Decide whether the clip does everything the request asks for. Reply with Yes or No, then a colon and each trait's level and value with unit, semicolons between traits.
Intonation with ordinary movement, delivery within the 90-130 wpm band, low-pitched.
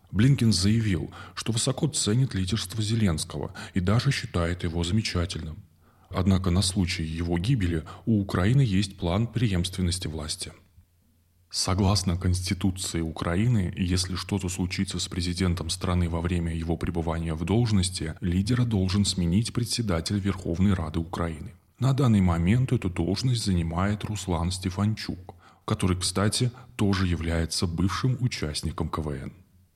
Yes: average, 3.5 semitones; average, 120 wpm; very low, 95 Hz